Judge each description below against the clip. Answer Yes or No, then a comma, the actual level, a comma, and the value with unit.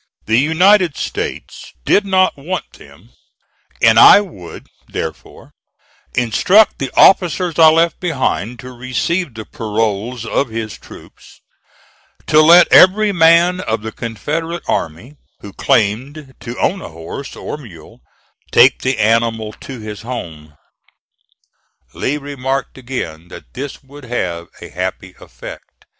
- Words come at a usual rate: No, slow, 130 wpm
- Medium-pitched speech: No, low, 130 Hz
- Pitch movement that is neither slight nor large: No, wide, 6.7 semitones